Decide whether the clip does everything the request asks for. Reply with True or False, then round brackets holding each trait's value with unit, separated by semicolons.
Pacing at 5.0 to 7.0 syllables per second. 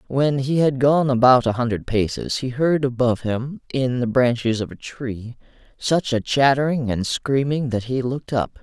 False (4.7 syllables/s)